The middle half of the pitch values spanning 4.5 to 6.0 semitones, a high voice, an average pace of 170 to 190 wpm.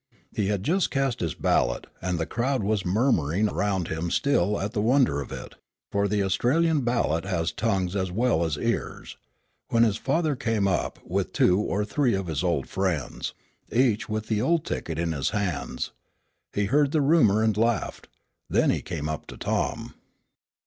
No: wide, 5.4 semitones; low, 105 Hz; average, 180 wpm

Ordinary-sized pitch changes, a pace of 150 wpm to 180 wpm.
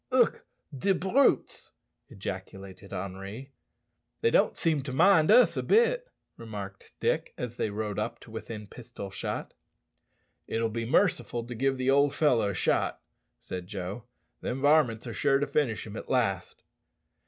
No: wide, 5.7 semitones; average, 155 wpm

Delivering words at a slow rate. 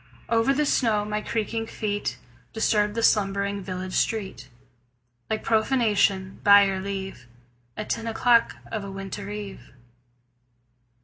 Yes: slow, 125 wpm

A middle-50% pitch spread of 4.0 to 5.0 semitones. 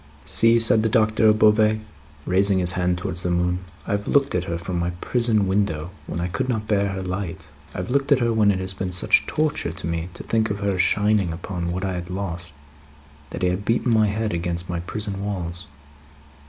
No: average, 3.4 semitones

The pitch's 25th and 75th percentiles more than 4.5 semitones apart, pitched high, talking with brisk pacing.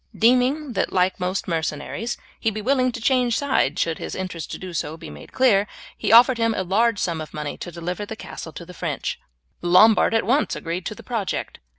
Yes: average, 5.3 semitones; high, 200 Hz; fast, 225 wpm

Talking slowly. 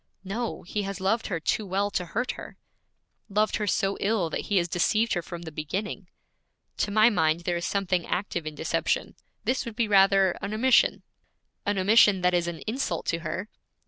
No: average, 195 wpm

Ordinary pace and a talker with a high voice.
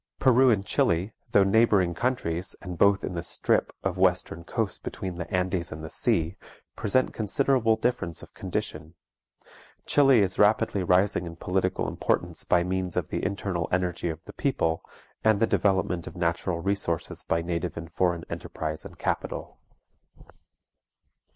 No: average, 150 wpm; very low, 90 Hz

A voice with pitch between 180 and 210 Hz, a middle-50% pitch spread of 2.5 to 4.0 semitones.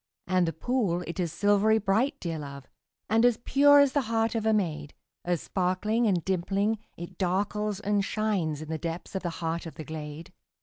No: high, 190 Hz; average, 4.6 semitones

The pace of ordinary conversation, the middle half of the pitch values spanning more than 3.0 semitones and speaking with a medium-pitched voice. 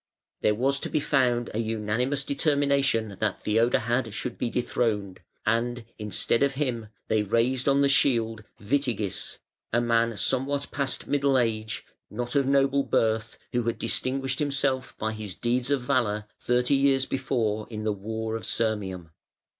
No: average, 155 wpm; average, 3.6 semitones; low, 120 Hz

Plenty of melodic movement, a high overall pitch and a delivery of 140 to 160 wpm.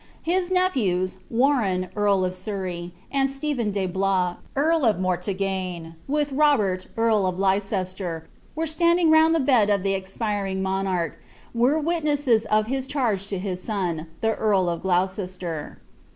Yes: wide, 6.6 semitones; high, 200 Hz; average, 150 wpm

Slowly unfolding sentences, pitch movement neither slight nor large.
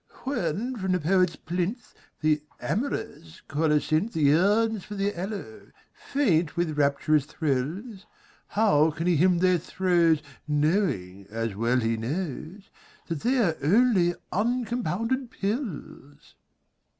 No: slow, 115 wpm; wide, 5.7 semitones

